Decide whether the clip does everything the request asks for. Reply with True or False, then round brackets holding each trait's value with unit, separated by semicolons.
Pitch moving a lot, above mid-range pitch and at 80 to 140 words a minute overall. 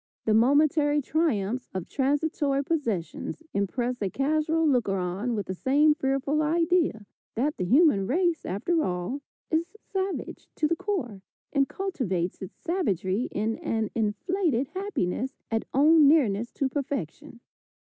True (6.8 semitones; 275 Hz; 135 wpm)